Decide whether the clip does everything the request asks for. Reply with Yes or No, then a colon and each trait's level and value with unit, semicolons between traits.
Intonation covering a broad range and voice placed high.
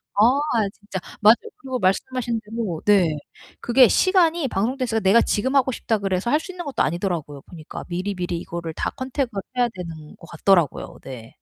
Yes: wide, 6.6 semitones; high, 210 Hz